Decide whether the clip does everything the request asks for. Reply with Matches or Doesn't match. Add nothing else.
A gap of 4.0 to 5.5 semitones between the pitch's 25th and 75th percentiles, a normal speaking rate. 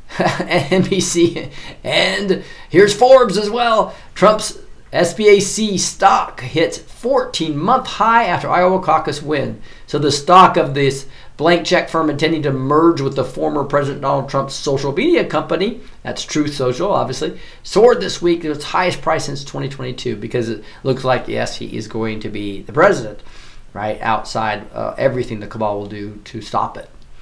Matches